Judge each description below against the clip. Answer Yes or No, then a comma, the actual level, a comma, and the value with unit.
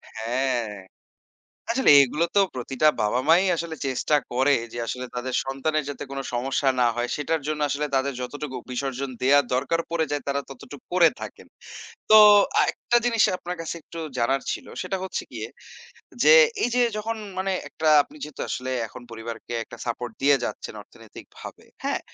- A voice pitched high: No, medium, 140 Hz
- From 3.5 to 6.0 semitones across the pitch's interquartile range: Yes, average, 4.2 semitones